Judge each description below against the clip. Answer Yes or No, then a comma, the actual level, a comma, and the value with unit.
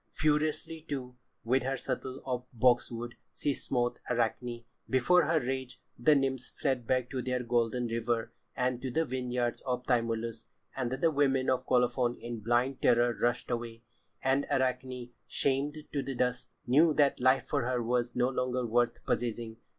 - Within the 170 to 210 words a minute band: No, average, 160 wpm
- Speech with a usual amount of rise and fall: No, narrow, 1.7 semitones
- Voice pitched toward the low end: Yes, low, 125 Hz